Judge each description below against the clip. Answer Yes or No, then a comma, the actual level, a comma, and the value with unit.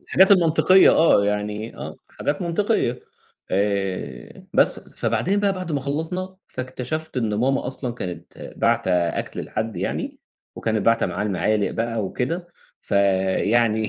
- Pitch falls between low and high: No, low, 115 Hz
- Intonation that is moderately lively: No, wide, 7.7 semitones